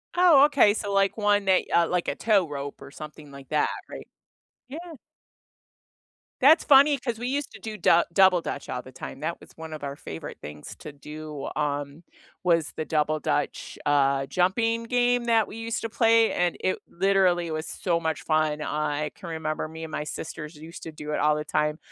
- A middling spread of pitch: No, wide, 6.2 semitones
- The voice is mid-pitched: Yes, medium, 165 Hz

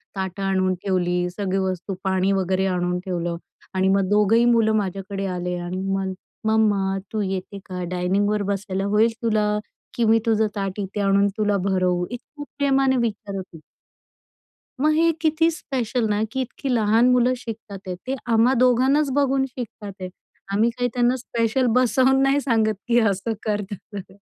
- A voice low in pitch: No, high, 210 Hz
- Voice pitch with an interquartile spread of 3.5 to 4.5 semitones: Yes, average, 4.1 semitones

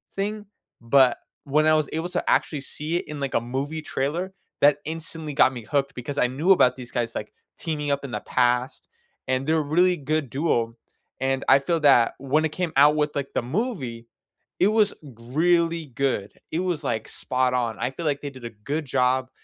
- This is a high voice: No, medium, 140 Hz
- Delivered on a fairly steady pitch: No, average, 3.8 semitones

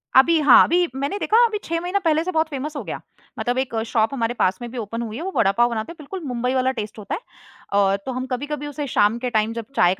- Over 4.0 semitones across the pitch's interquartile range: Yes, wide, 5.4 semitones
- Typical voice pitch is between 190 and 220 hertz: No, very high, 255 Hz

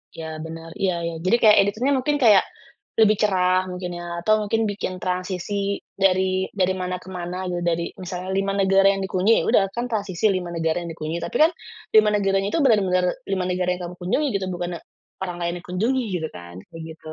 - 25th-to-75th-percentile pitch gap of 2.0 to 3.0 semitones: Yes, narrow, 2.4 semitones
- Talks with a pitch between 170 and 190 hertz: Yes, medium, 185 Hz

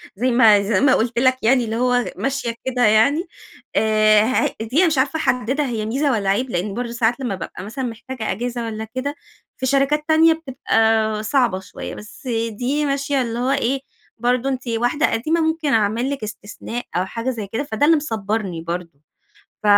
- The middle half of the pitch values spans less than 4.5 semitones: Yes, average, 3.8 semitones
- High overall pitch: Yes, high, 240 Hz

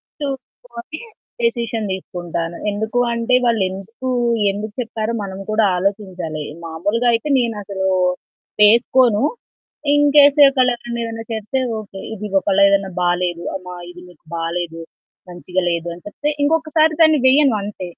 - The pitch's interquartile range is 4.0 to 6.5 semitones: Yes, average, 4.8 semitones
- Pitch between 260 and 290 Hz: No, high, 215 Hz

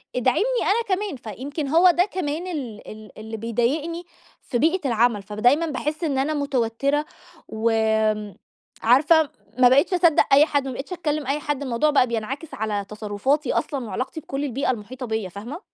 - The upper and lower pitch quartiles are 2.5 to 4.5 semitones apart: No, average, 5.2 semitones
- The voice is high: Yes, very high, 270 Hz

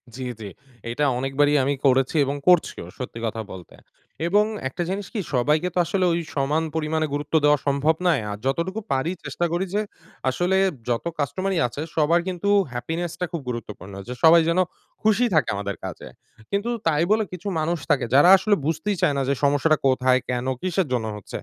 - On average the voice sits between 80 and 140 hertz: No, medium, 155 Hz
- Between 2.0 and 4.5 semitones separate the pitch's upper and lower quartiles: No, average, 5.1 semitones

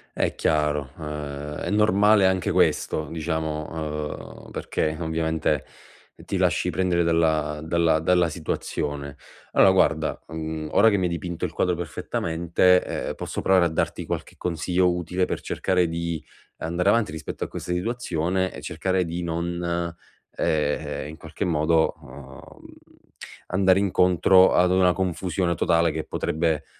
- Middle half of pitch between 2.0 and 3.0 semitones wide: Yes, narrow, 2.6 semitones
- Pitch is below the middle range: Yes, very low, 85 Hz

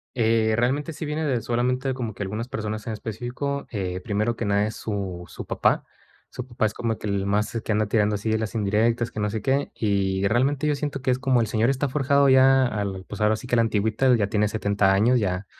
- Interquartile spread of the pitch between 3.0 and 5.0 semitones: Yes, average, 3.6 semitones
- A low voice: Yes, low, 110 Hz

